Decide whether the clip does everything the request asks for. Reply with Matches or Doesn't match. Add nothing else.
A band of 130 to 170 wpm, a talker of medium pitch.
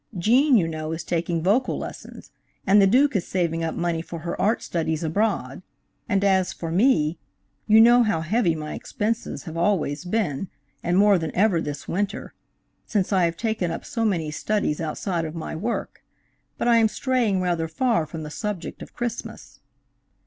Doesn't match